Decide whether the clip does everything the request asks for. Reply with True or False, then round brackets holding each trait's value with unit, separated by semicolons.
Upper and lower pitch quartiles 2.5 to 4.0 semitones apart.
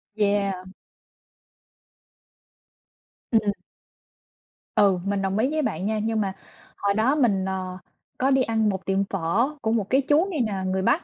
True (3.7 semitones)